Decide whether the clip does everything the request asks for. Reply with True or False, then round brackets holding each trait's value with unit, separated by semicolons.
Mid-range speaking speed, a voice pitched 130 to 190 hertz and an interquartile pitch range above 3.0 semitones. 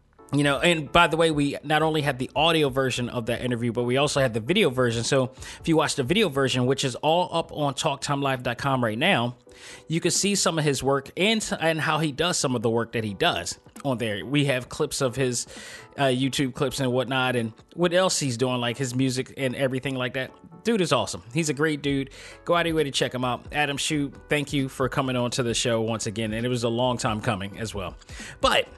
False (250 wpm; 135 Hz; 3.7 semitones)